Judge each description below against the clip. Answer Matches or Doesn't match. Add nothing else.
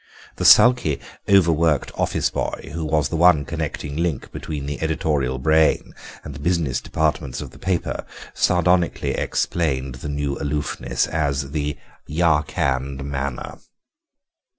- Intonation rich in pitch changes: Doesn't match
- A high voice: Doesn't match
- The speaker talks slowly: Matches